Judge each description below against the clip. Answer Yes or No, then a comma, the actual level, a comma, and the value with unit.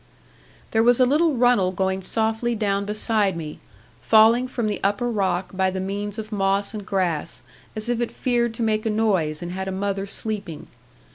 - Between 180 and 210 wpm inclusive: Yes, average, 190 wpm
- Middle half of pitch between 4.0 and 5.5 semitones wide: No, average, 3.0 semitones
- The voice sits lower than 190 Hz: No, high, 210 Hz